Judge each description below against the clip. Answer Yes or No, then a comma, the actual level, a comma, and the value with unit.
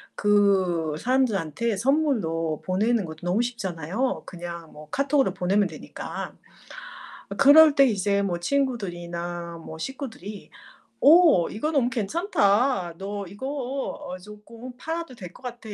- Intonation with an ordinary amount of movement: No, wide, 6.6 semitones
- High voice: Yes, high, 205 Hz